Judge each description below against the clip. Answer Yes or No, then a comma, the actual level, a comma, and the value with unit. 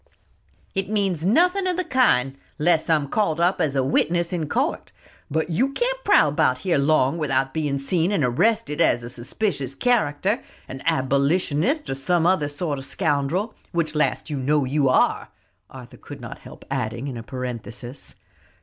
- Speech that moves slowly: No, average, 170 wpm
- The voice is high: No, medium, 155 Hz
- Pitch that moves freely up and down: Yes, wide, 5.7 semitones